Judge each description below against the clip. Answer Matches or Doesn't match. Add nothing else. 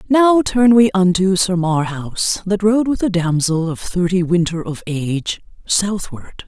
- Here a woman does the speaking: Matches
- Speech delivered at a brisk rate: Doesn't match